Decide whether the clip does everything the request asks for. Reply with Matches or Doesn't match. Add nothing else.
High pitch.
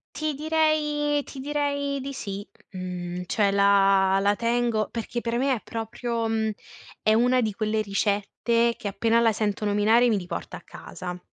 Matches